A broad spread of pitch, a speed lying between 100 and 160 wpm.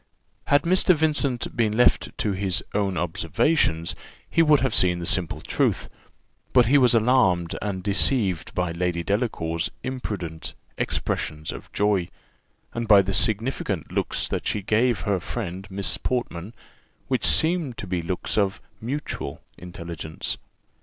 Yes: wide, 5.9 semitones; average, 140 wpm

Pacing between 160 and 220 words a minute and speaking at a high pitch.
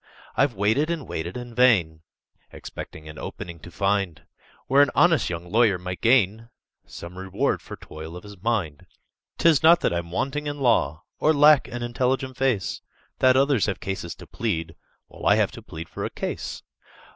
No: average, 180 wpm; low, 110 Hz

